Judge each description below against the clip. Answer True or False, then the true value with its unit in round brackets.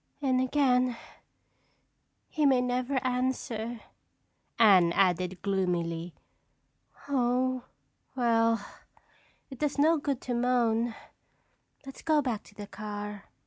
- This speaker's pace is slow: True (100 wpm)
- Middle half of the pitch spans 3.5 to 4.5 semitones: True (3.9 semitones)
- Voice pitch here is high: True (240 Hz)